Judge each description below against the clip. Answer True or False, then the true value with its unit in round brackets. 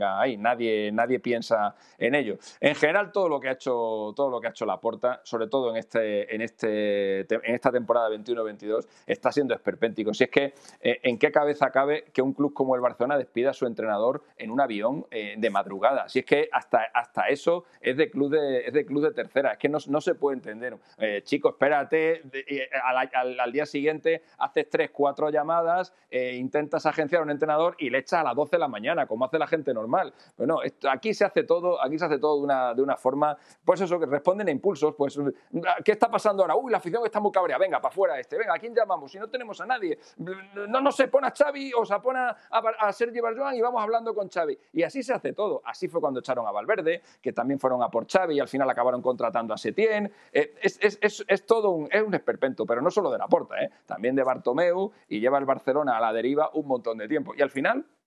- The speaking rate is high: True (245 wpm)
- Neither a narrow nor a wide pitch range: False (8.4 semitones)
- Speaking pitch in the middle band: True (150 Hz)